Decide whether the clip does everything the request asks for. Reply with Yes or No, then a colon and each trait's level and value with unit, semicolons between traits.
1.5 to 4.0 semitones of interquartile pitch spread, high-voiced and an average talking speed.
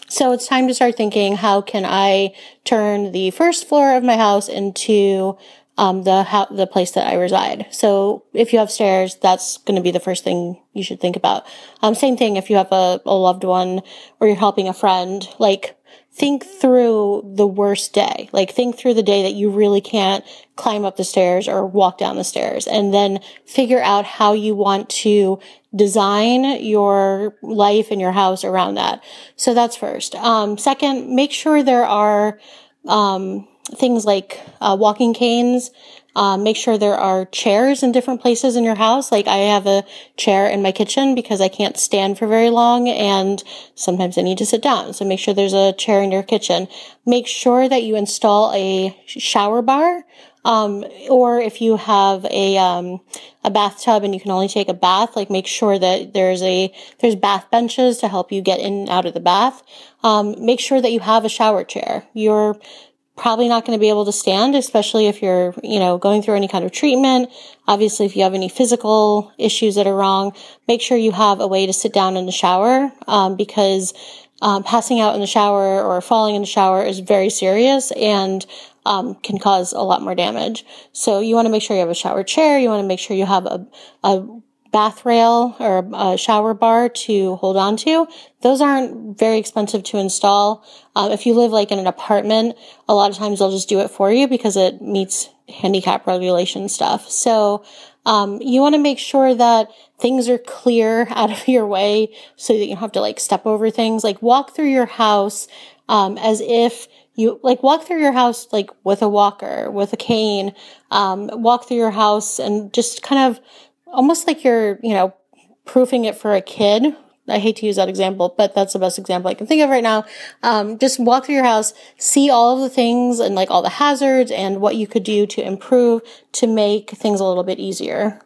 No: average, 3.5 semitones; high, 210 Hz; fast, 210 wpm